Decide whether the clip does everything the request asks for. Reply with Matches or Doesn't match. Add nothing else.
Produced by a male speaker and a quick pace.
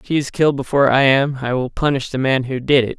Matches